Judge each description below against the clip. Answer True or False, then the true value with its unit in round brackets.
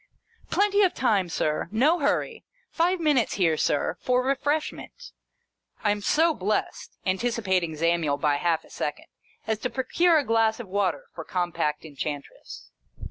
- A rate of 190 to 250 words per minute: False (150 wpm)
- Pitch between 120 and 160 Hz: False (215 Hz)